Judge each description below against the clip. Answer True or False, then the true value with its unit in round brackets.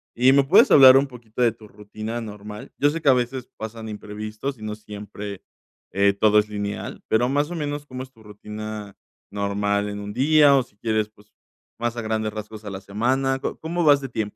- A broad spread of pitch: False (3.9 semitones)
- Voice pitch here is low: True (110 Hz)